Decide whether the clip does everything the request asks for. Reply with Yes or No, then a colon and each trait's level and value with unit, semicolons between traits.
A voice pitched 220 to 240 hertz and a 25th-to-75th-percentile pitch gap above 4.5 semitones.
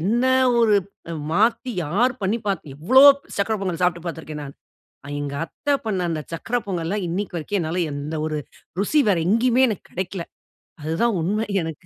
No: medium, 185 Hz; average, 5.2 semitones